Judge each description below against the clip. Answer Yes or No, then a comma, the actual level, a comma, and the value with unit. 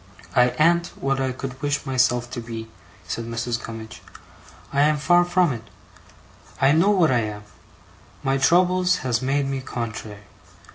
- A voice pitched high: No, low, 135 Hz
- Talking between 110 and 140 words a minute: No, average, 155 wpm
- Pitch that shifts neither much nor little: Yes, average, 4.6 semitones